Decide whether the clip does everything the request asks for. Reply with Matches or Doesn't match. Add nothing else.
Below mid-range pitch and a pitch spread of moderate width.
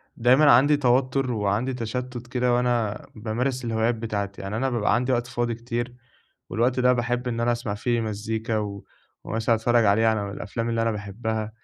Doesn't match